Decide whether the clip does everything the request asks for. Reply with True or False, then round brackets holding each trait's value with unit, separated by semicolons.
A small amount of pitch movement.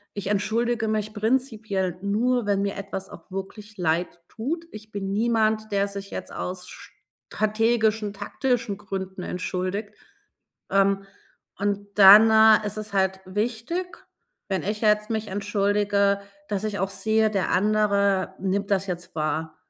True (1.9 semitones)